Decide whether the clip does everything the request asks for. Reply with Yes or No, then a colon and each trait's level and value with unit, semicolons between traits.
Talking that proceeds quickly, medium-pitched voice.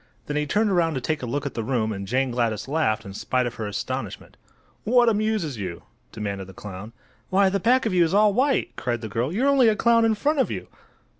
Yes: fast, 240 wpm; medium, 145 Hz